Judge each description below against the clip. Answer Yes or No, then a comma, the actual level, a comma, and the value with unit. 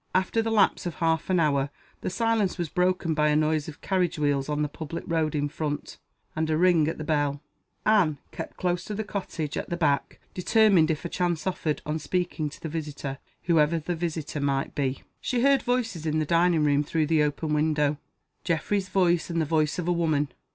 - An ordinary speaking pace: No, fast, 210 wpm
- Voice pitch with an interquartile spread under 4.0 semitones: Yes, average, 3.0 semitones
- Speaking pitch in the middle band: Yes, medium, 160 Hz